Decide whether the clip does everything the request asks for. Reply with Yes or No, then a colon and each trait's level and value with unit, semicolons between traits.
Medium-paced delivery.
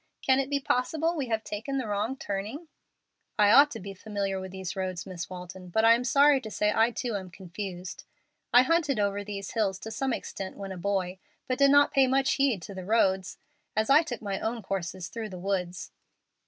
No: fast, 215 wpm